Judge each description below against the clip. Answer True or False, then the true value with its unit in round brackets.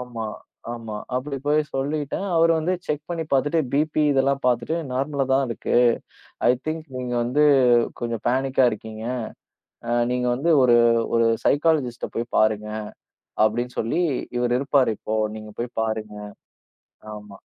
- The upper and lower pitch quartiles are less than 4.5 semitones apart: True (4.0 semitones)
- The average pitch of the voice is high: False (125 Hz)